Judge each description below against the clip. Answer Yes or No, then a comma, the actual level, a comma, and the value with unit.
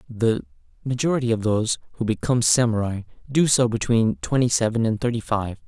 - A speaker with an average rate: Yes, average, 160 wpm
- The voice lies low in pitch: Yes, low, 115 Hz